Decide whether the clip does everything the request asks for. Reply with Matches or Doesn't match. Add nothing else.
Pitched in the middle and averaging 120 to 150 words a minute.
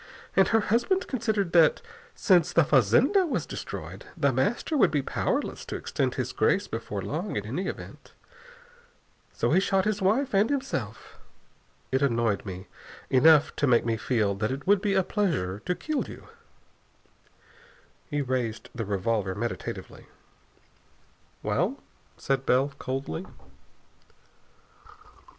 Matches